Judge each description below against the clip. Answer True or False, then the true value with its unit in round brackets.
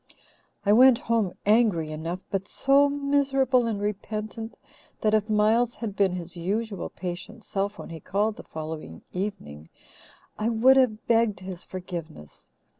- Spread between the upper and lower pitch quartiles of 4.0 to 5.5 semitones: True (4.3 semitones)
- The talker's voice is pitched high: True (210 Hz)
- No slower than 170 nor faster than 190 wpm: False (145 wpm)